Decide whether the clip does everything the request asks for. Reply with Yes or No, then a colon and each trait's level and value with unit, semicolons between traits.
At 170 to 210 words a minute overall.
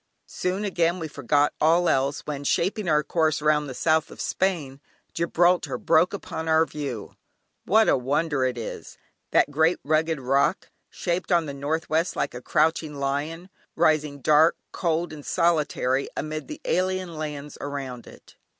No: average, 155 wpm